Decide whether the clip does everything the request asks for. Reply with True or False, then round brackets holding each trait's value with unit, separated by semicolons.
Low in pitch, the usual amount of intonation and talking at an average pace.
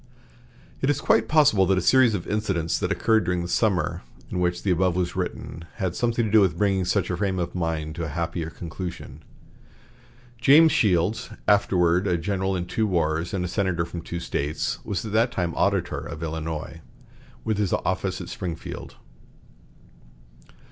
True (90 Hz; 3.4 semitones; 175 wpm)